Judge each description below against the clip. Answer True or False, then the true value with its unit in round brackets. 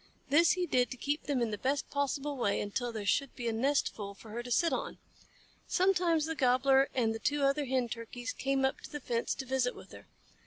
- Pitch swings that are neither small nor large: True (3.3 semitones)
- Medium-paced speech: False (230 wpm)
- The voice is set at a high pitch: True (265 Hz)